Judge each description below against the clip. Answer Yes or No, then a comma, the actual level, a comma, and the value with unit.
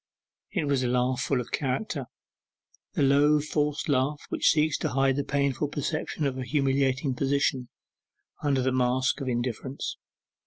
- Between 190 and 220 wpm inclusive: No, average, 155 wpm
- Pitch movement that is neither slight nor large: No, narrow, 2.0 semitones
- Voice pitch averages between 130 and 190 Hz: Yes, low, 135 Hz